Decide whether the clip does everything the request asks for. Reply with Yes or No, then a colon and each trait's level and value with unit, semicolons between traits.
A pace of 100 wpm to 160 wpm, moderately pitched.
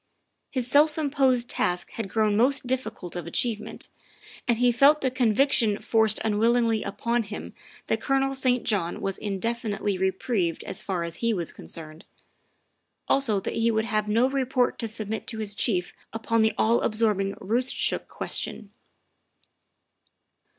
No: average, 145 wpm; high, 225 Hz